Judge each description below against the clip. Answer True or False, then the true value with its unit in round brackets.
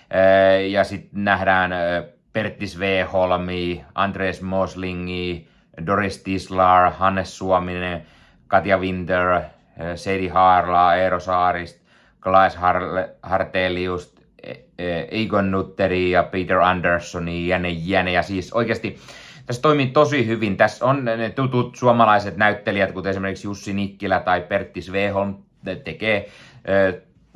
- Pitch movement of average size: False (1.7 semitones)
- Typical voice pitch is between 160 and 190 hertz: False (95 Hz)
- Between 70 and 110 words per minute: True (105 wpm)